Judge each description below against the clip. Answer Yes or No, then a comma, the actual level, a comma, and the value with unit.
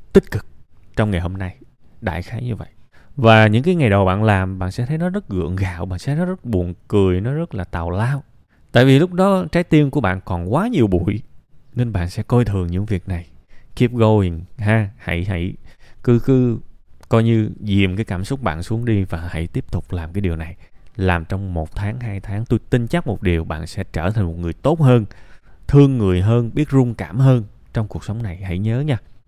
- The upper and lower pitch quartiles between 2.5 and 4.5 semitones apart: No, average, 5.1 semitones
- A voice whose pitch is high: No, low, 105 Hz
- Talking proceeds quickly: No, average, 230 wpm